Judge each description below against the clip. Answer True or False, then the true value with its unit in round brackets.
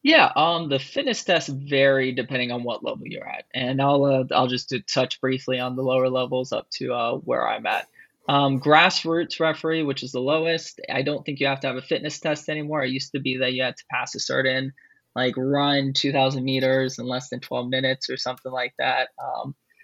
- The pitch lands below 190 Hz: True (135 Hz)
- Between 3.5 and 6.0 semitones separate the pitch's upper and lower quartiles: False (2.7 semitones)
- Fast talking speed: True (220 wpm)